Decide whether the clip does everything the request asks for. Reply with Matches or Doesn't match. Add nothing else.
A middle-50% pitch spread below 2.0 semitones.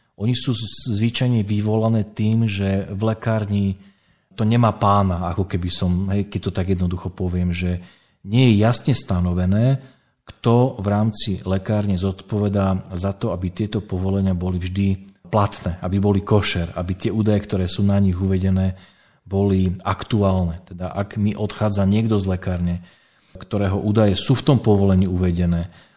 Doesn't match